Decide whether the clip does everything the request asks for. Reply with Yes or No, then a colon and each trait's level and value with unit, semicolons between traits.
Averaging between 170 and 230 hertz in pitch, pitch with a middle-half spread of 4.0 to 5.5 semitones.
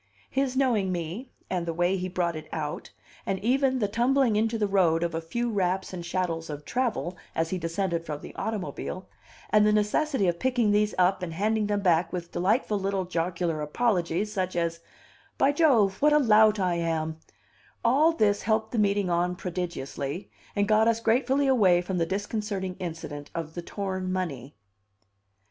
Yes: high, 190 Hz; average, 4.3 semitones